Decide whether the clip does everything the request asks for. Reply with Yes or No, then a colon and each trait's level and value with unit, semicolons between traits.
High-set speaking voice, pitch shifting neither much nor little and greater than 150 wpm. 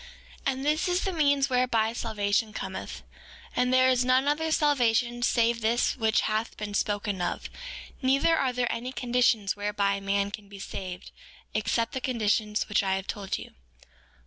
Yes: high, 230 Hz; average, 3.8 semitones; average, 170 wpm